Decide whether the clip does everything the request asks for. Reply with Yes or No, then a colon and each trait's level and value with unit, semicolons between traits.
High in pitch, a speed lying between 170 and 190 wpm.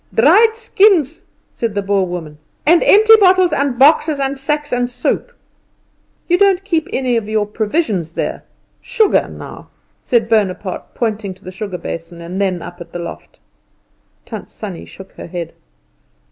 No: high, 230 Hz; average, 160 wpm